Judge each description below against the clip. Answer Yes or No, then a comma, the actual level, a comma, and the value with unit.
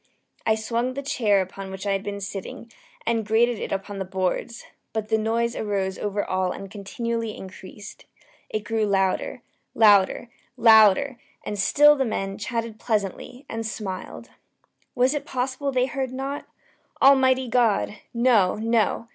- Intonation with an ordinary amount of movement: Yes, average, 3.5 semitones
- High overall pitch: Yes, high, 220 Hz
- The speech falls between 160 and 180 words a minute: No, average, 150 wpm